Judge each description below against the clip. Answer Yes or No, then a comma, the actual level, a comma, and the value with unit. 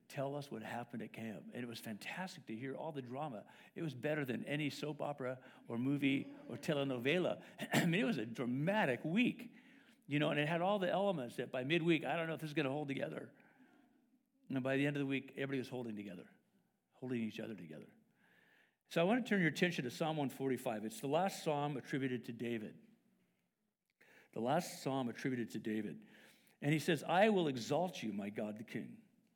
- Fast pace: Yes, fast, 210 wpm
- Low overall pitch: No, medium, 145 Hz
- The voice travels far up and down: Yes, wide, 6.4 semitones